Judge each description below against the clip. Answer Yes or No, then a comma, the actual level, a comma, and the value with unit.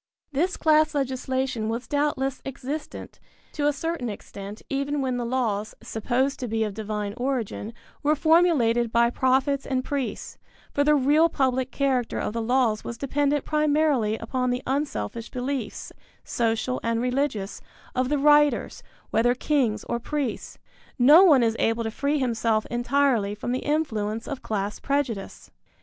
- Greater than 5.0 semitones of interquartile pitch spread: No, average, 3.9 semitones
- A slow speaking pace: No, average, 150 wpm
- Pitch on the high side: Yes, very high, 255 Hz